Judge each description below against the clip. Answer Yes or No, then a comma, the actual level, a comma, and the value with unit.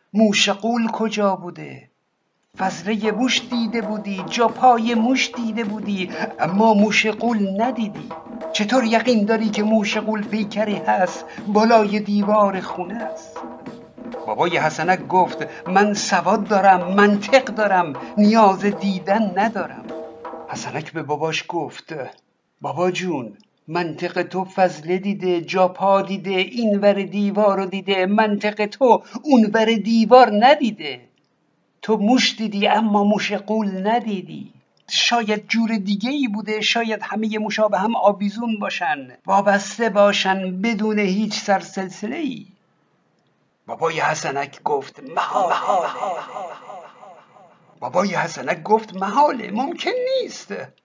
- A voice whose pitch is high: Yes, high, 210 Hz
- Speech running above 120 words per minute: No, average, 115 wpm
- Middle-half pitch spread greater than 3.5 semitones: No, average, 2.8 semitones